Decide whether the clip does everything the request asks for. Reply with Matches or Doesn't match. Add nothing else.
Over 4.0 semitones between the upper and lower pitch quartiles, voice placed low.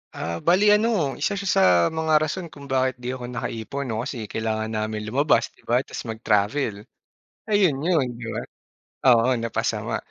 Matches